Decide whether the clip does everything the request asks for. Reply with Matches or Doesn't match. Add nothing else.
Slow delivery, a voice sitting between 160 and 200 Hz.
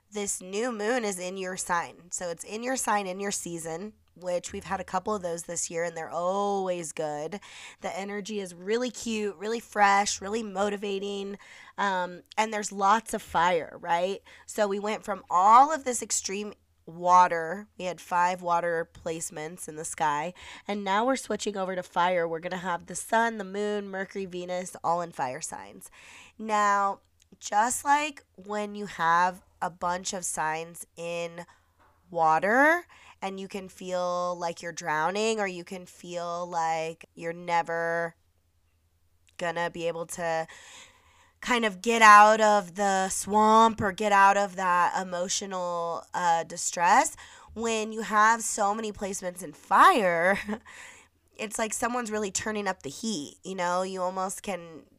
Doesn't match